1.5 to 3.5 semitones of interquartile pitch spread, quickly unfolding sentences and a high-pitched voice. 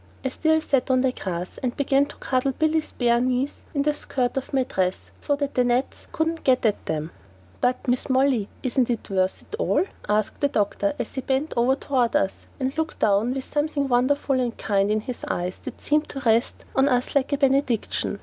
Yes: average, 3.1 semitones; fast, 210 wpm; very high, 260 Hz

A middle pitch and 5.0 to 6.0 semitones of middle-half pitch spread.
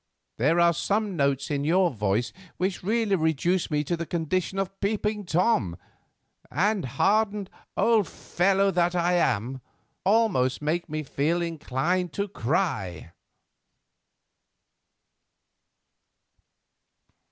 Yes: medium, 175 Hz; wide, 5.5 semitones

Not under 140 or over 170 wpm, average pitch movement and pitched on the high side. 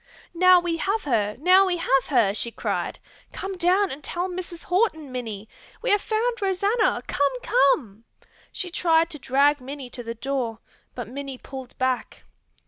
No: average, 165 wpm; wide, 6.4 semitones; very high, 290 Hz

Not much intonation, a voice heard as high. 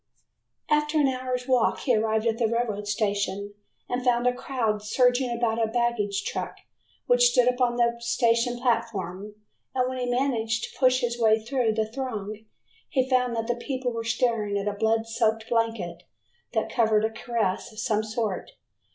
Yes: narrow, 2.3 semitones; high, 230 Hz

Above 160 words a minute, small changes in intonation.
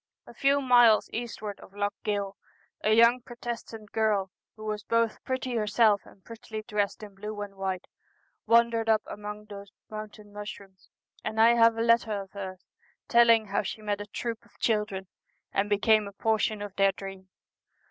Yes: average, 170 wpm; narrow, 2.1 semitones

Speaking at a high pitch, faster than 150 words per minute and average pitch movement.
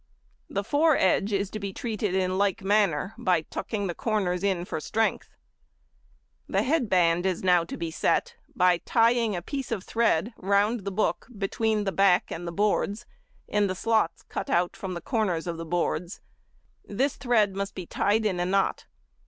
Yes: high, 200 Hz; average, 180 wpm; average, 3.5 semitones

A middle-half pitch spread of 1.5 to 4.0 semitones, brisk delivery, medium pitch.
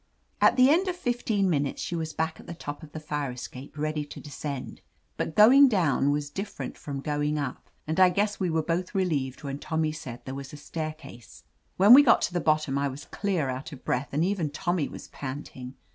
No: average, 4.4 semitones; fast, 220 wpm; medium, 155 Hz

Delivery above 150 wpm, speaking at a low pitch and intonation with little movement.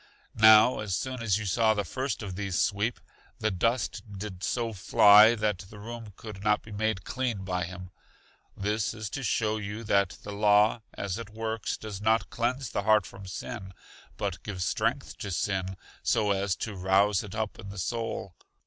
Yes: average, 185 wpm; low, 105 Hz; narrow, 2.3 semitones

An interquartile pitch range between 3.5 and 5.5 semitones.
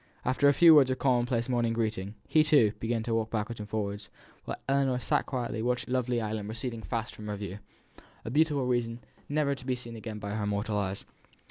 No: average, 3.1 semitones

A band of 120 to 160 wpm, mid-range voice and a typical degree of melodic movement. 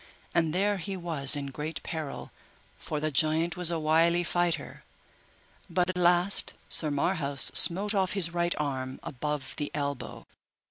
Yes: average, 150 wpm; medium, 165 Hz; average, 3.1 semitones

